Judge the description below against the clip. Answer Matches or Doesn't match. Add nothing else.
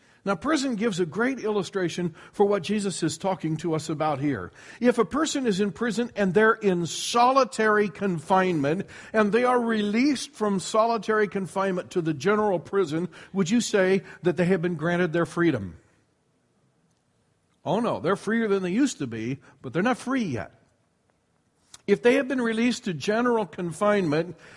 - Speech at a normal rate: Matches